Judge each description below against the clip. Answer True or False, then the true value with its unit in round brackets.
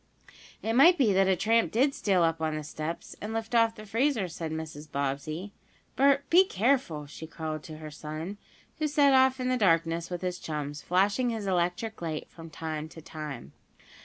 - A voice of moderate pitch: True (180 Hz)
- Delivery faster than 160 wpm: True (190 wpm)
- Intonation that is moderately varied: False (6.4 semitones)